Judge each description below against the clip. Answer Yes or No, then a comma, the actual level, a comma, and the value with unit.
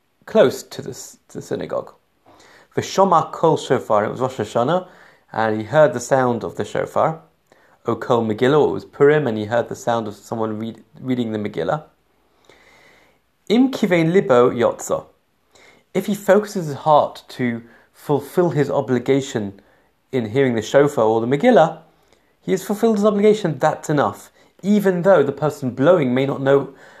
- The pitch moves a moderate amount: No, wide, 7.3 semitones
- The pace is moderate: Yes, average, 160 wpm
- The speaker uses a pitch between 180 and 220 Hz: No, medium, 140 Hz